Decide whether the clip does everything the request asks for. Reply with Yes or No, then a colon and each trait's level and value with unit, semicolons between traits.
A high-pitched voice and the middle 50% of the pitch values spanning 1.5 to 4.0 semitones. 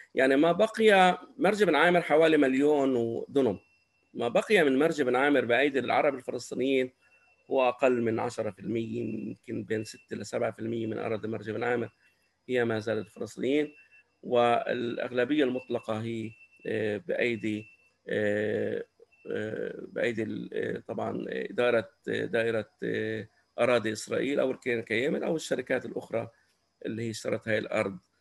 No: low, 120 Hz; average, 3.3 semitones